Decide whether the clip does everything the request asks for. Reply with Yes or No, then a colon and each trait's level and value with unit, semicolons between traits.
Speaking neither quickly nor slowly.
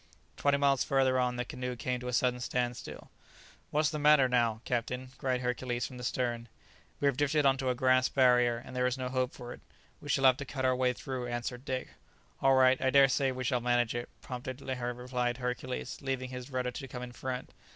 No: fast, 220 wpm